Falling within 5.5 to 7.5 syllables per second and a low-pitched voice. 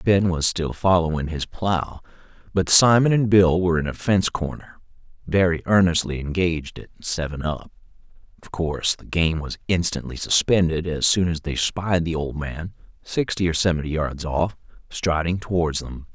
No: 4.9 syllables/s; very low, 85 Hz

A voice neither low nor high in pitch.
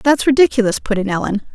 No: high, 235 Hz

